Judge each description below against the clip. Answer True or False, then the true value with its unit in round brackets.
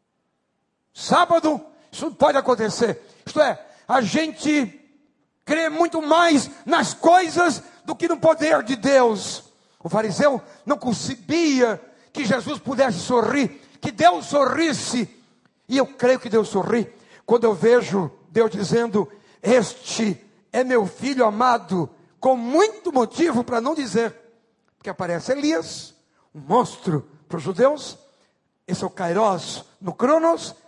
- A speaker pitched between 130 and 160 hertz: False (245 Hz)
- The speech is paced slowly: False (130 wpm)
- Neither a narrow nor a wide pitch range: False (5.8 semitones)